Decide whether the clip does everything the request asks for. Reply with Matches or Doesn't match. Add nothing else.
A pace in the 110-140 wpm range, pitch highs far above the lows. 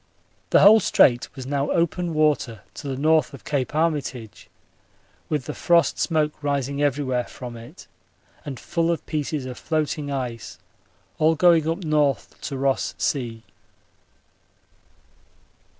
Doesn't match